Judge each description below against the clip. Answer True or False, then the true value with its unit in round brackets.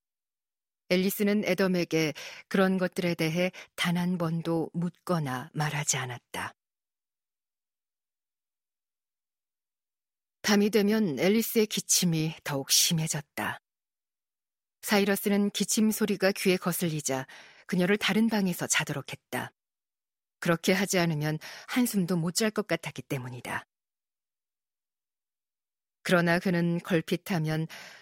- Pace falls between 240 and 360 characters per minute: False (225 characters per minute)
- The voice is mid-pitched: True (180 Hz)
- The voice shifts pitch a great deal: False (4.0 semitones)